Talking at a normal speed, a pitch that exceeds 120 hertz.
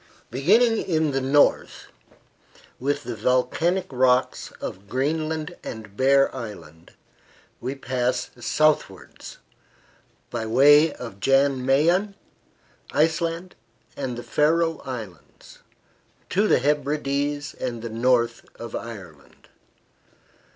No: slow, 100 wpm; low, 135 Hz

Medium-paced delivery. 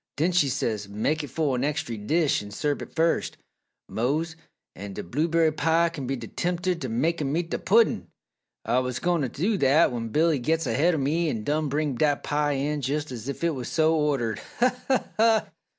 No: fast, 215 wpm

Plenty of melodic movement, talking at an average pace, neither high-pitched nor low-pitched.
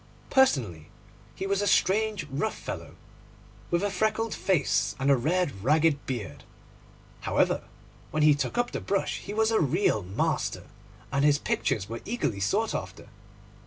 Yes: wide, 7.7 semitones; average, 155 wpm; medium, 155 Hz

